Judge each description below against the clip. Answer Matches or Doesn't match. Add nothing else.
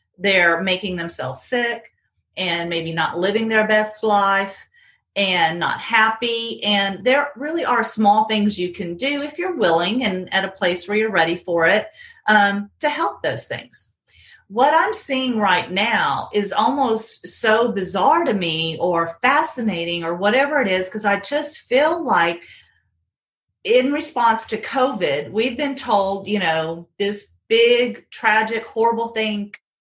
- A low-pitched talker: Doesn't match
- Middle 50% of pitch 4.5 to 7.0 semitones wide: Matches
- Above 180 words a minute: Doesn't match